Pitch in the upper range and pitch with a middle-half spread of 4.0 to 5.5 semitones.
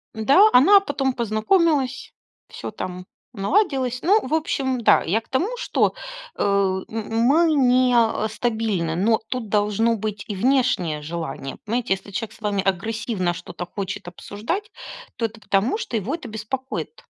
Yes: high, 225 Hz; average, 4.8 semitones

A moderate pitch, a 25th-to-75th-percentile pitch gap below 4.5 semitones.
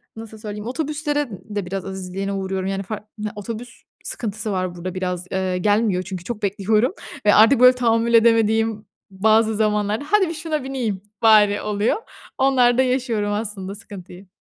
No: high, 215 Hz; average, 3.2 semitones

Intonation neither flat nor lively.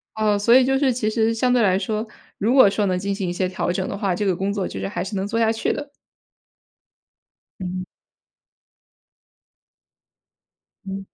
Yes: average, 3.2 semitones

